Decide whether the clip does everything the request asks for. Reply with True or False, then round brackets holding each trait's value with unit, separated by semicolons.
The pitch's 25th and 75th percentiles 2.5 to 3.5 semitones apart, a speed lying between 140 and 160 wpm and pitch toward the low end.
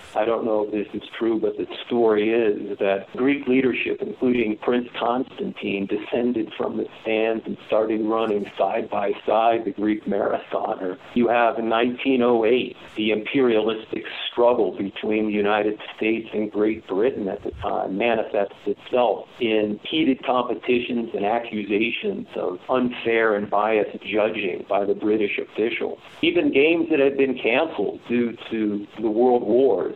True (2.9 semitones; 150 wpm; 115 Hz)